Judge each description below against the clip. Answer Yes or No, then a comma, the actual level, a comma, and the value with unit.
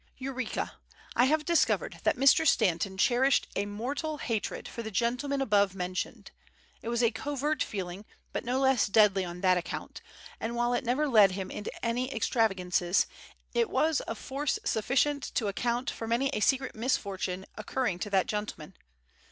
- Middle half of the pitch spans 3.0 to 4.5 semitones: No, average, 5.1 semitones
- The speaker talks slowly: No, average, 165 wpm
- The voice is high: Yes, high, 230 Hz